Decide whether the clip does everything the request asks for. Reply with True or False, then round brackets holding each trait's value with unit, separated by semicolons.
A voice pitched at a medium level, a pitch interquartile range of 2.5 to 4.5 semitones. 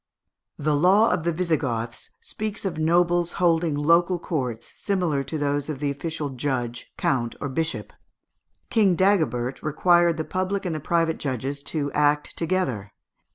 True (155 Hz; 3.7 semitones)